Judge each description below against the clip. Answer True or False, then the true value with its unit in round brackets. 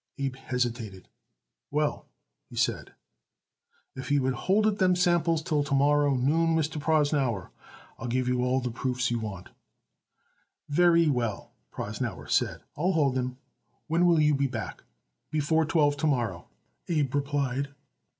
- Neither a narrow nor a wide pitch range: True (3.9 semitones)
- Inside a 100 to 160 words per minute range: True (145 wpm)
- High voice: False (145 Hz)